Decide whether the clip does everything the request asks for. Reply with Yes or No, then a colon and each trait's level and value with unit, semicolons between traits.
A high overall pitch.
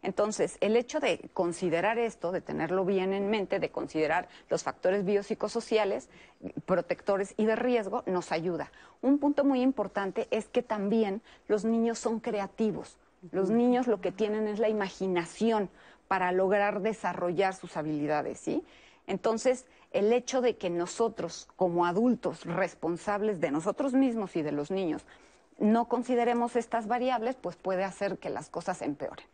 Yes: high, 205 Hz